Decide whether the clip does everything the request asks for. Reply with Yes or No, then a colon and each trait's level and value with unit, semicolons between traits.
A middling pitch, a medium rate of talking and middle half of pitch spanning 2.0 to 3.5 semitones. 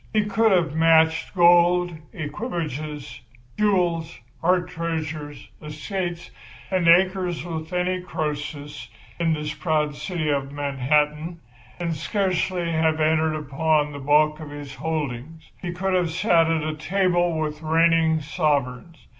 No: medium, 160 Hz; slow, 125 wpm; average, 2.7 semitones